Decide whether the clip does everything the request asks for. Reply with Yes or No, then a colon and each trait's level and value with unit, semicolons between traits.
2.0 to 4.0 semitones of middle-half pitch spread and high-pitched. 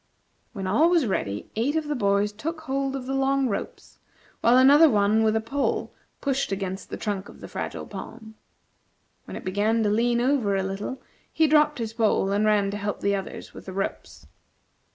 No: average, 5.2 semitones; high, 220 Hz